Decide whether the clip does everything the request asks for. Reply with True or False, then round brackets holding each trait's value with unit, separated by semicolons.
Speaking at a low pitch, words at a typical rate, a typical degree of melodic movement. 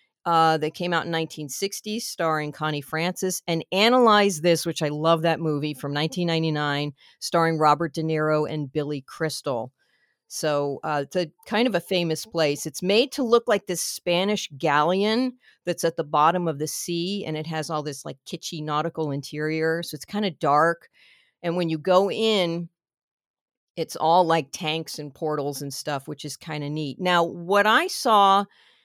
False (165 Hz; 180 wpm; 3.0 semitones)